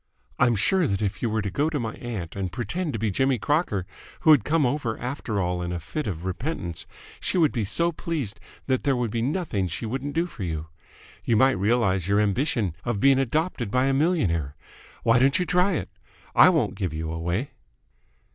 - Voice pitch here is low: Yes, low, 120 Hz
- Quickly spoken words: Yes, fast, 210 wpm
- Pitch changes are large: Yes, wide, 6.8 semitones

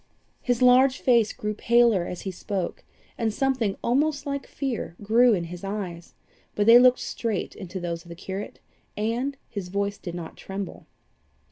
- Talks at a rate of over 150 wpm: Yes, average, 165 wpm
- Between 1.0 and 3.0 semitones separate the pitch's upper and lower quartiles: No, average, 4.8 semitones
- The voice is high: Yes, high, 210 Hz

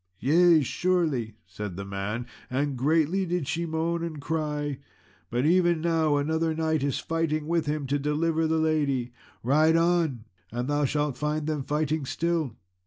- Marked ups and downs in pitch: No, average, 2.8 semitones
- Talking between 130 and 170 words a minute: Yes, average, 160 wpm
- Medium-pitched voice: Yes, medium, 155 Hz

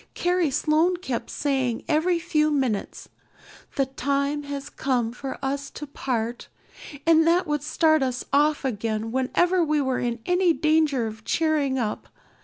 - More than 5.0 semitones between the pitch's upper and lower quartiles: No, average, 3.6 semitones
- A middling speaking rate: Yes, average, 150 wpm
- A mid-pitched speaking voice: No, very high, 280 Hz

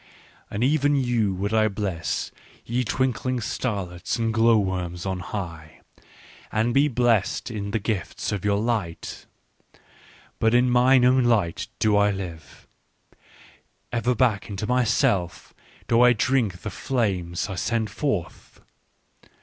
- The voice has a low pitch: Yes, low, 110 Hz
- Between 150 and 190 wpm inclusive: No, average, 140 wpm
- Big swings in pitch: No, average, 4.2 semitones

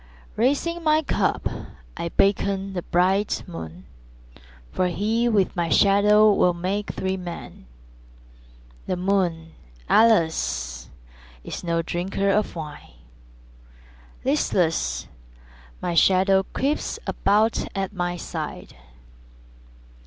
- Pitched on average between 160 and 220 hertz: Yes, high, 190 Hz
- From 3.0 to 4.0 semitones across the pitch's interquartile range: Yes, average, 3.4 semitones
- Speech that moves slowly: Yes, slow, 100 wpm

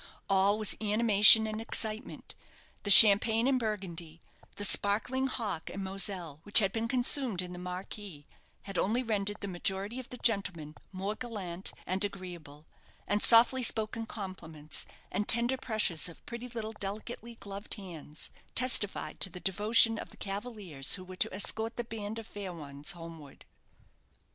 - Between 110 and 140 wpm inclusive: No, average, 155 wpm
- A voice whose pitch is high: Yes, high, 205 Hz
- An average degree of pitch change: Yes, average, 3.6 semitones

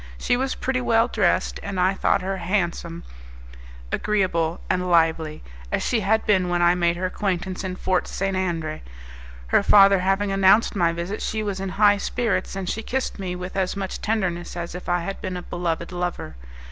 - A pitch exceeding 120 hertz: Yes, medium, 185 Hz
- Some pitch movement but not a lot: No, narrow, 2.3 semitones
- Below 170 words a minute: No, average, 190 wpm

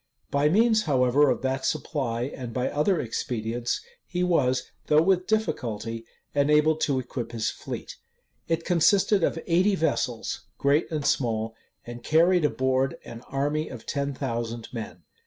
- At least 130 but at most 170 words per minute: Yes, average, 150 wpm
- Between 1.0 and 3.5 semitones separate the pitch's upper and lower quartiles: No, average, 5.2 semitones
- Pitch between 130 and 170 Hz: Yes, medium, 140 Hz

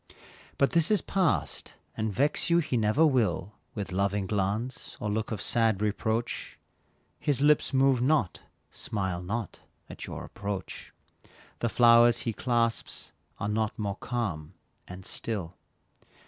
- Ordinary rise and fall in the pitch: Yes, average, 4.2 semitones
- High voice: No, low, 110 Hz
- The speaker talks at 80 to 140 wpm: Yes, slow, 135 wpm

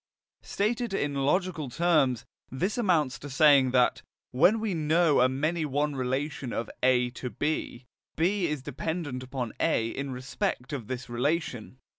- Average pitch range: Yes, average, 4.5 semitones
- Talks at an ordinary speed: Yes, average, 150 wpm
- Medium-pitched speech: Yes, medium, 145 Hz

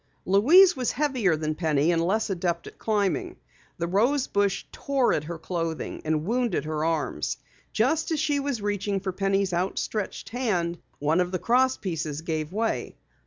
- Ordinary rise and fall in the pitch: No, wide, 6.7 semitones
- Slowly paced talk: No, average, 165 wpm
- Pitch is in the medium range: No, high, 195 Hz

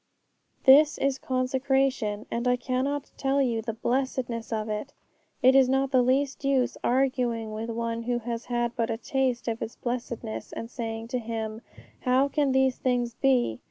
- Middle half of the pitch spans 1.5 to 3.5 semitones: Yes, narrow, 2.6 semitones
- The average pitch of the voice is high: Yes, high, 245 Hz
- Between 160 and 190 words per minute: Yes, average, 170 wpm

